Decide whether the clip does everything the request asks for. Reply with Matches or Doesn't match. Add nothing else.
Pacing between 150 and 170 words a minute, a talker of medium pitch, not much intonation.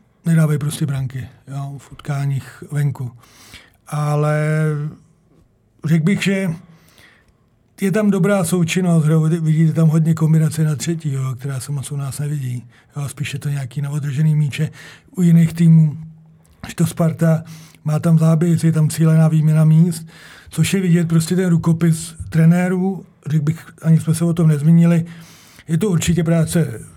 Matches